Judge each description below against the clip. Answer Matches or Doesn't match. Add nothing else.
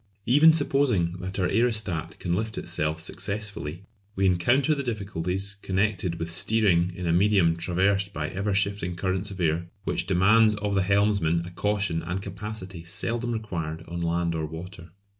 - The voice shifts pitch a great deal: Doesn't match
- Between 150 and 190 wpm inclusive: Matches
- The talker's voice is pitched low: Matches